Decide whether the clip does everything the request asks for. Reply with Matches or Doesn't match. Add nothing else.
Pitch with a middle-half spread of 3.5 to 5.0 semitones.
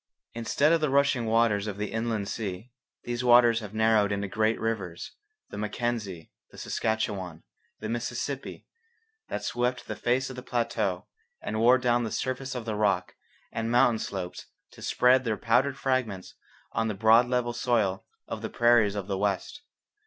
Doesn't match